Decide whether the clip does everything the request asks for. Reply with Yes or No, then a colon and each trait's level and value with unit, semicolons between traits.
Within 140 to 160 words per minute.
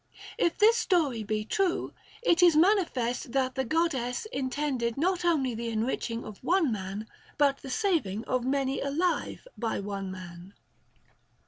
Yes: average, 150 wpm